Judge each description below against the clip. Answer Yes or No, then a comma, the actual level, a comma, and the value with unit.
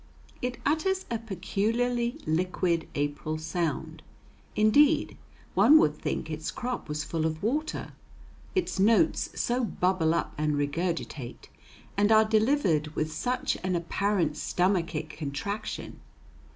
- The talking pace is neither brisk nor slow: No, slow, 120 wpm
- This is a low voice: No, medium, 185 Hz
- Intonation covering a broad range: Yes, wide, 6.8 semitones